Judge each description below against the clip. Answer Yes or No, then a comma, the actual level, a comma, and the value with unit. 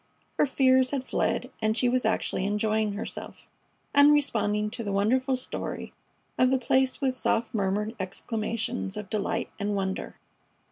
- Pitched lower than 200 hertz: No, high, 225 Hz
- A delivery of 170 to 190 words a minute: No, average, 150 wpm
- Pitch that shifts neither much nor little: Yes, average, 3.7 semitones